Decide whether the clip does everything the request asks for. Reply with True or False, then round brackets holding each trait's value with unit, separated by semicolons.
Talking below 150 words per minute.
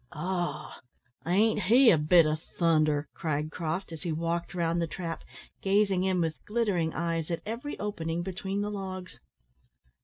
False (155 wpm)